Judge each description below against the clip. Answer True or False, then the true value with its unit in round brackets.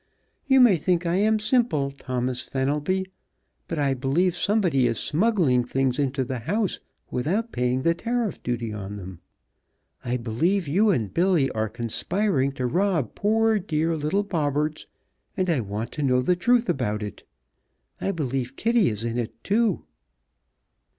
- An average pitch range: False (7.6 semitones)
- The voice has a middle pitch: True (150 Hz)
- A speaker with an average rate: True (155 wpm)